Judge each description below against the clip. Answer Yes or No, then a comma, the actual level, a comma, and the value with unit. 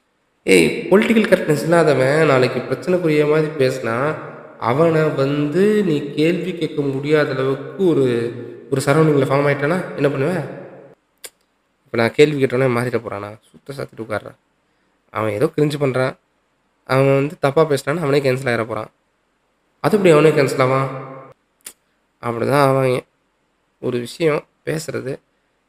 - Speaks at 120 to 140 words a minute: Yes, average, 125 wpm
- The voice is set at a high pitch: No, medium, 140 Hz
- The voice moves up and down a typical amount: Yes, average, 3.2 semitones